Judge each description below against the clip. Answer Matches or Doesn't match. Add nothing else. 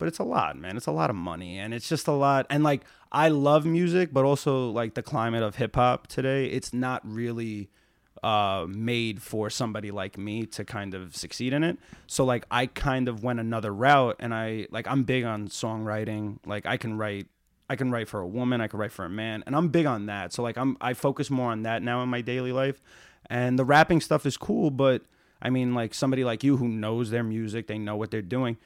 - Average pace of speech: Doesn't match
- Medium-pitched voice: Doesn't match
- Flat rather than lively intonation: Doesn't match